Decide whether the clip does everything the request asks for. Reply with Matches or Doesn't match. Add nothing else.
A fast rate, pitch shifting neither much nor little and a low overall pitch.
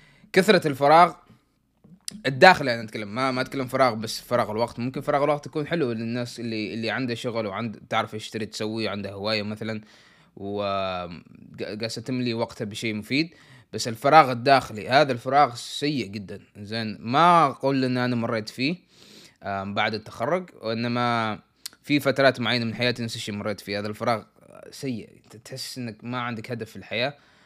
Matches